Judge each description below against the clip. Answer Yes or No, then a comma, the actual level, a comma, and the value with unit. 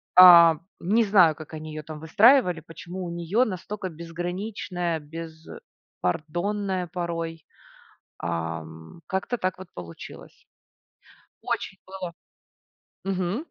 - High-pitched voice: No, medium, 175 Hz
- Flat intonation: No, average, 3.0 semitones